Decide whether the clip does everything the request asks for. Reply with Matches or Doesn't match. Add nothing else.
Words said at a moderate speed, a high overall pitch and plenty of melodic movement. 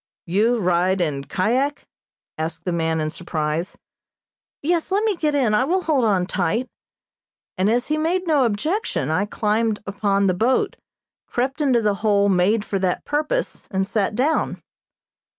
Matches